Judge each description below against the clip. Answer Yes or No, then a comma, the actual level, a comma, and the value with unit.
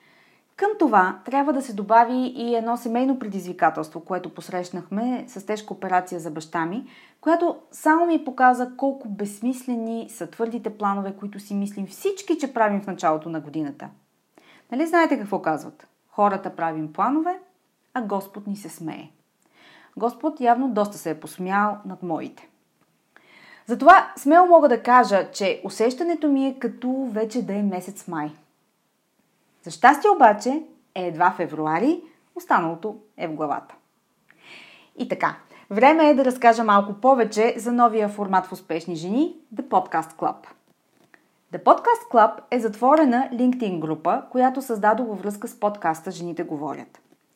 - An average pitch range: No, wide, 6.1 semitones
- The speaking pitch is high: Yes, high, 220 Hz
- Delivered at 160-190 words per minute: No, average, 145 wpm